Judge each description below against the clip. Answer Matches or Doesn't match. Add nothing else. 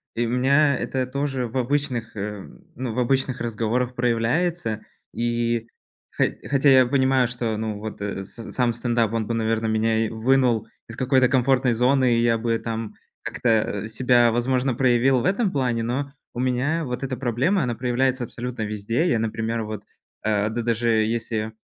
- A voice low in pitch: Matches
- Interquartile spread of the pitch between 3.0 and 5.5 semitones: Doesn't match